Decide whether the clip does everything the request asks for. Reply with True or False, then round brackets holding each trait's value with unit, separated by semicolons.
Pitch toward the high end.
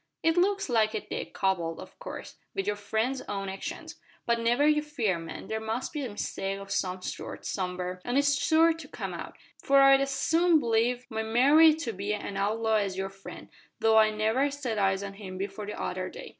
True (220 Hz)